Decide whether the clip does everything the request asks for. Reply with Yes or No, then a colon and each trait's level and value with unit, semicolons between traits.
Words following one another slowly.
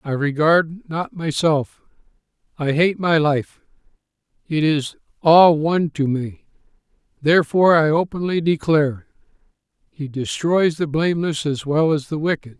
Yes: slow, 130 wpm